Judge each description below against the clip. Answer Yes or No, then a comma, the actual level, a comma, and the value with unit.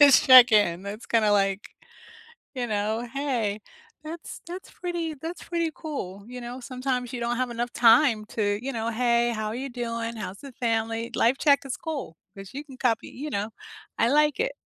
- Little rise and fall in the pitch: No, average, 3.9 semitones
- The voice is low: No, high, 240 Hz